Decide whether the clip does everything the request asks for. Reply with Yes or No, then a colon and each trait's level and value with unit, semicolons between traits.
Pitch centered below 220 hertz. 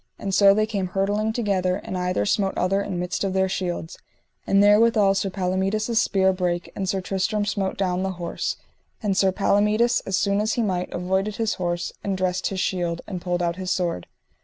Yes: high, 190 Hz